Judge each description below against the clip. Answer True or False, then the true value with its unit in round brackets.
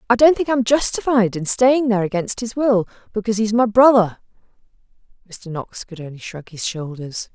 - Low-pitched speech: False (210 Hz)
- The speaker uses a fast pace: False (195 wpm)